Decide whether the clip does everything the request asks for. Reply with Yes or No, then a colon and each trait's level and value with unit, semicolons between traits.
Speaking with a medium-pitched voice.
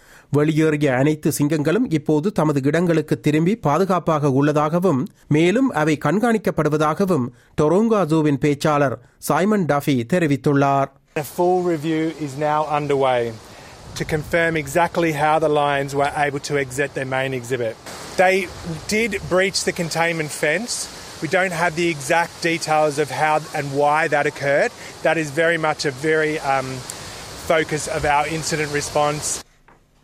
Yes: medium, 155 Hz